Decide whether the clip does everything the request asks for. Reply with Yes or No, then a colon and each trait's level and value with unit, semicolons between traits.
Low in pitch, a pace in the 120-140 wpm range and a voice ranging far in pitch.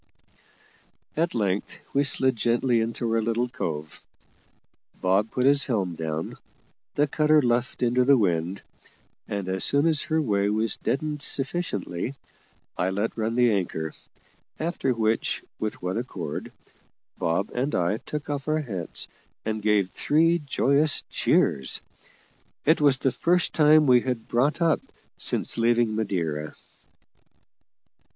Yes: low, 120 Hz; slow, 135 wpm; wide, 6.1 semitones